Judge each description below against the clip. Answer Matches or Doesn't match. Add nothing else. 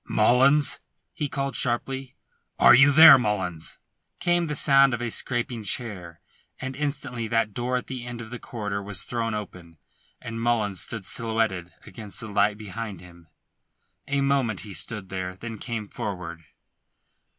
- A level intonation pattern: Doesn't match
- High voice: Doesn't match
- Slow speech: Doesn't match